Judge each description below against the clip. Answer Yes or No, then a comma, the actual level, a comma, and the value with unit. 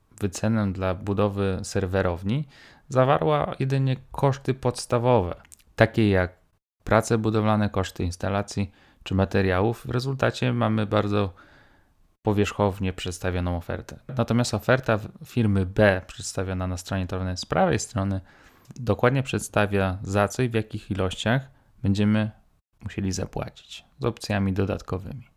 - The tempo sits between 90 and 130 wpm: Yes, average, 115 wpm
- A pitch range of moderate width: Yes, average, 3.7 semitones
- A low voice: Yes, low, 105 Hz